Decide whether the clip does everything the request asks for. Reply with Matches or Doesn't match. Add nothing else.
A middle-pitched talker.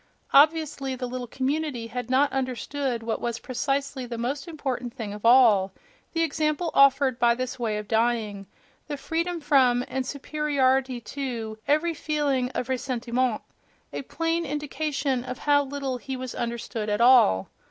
Doesn't match